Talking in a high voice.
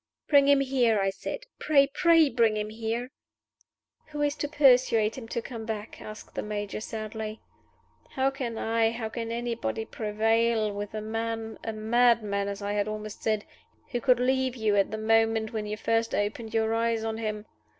Yes: high, 225 Hz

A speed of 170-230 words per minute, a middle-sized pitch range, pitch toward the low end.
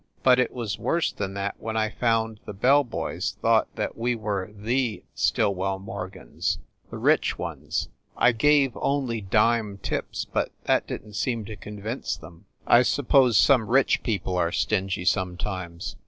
No: average, 160 wpm; average, 3.8 semitones; low, 110 Hz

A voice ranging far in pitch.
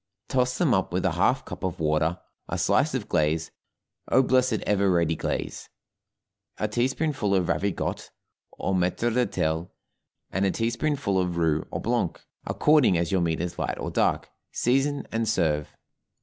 Yes: wide, 6.7 semitones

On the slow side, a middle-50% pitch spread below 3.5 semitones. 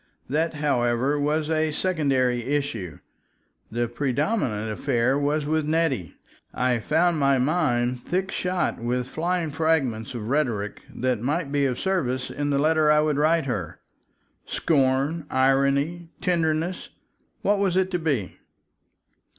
No: slow, 130 wpm; average, 4.2 semitones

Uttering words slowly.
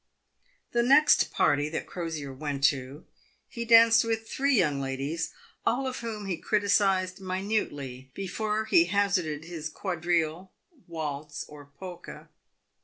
Yes: slow, 125 wpm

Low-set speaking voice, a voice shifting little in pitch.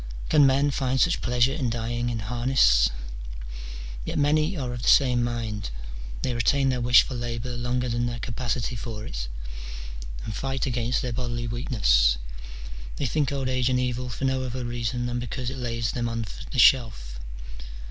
Yes: low, 120 Hz; narrow, 1.8 semitones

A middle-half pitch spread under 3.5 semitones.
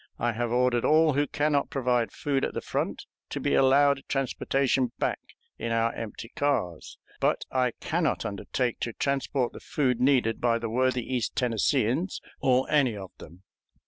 Yes: average, 3.0 semitones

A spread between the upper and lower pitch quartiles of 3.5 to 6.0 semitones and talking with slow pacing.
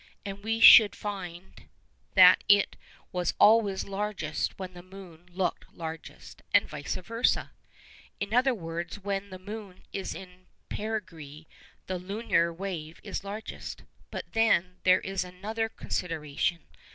No: average, 2.8 semitones; slow, 130 wpm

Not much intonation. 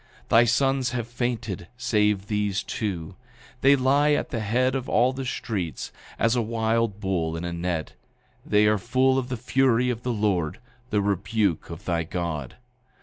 No: average, 4.5 semitones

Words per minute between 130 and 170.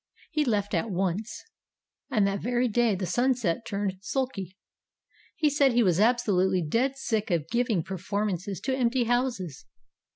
Yes: average, 155 wpm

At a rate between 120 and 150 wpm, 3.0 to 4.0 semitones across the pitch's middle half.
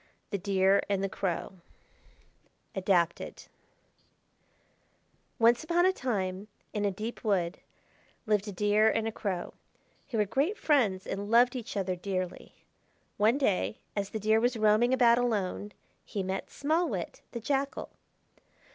Yes: average, 140 wpm; average, 3.7 semitones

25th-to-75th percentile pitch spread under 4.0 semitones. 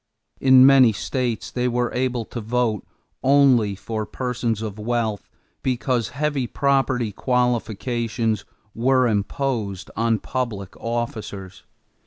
Yes: average, 2.8 semitones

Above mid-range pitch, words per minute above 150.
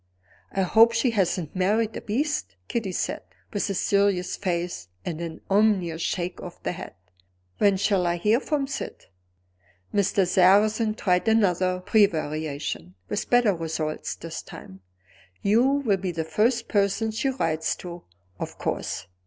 No: high, 195 Hz; average, 145 wpm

